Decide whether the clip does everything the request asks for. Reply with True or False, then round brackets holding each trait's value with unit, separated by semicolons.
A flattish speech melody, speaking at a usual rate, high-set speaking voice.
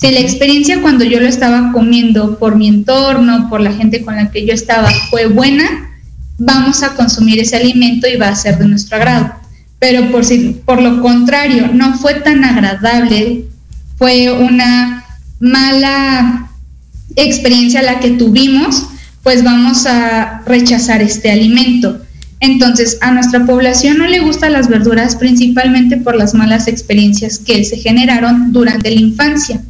True (2.1 semitones; 155 wpm; 245 Hz)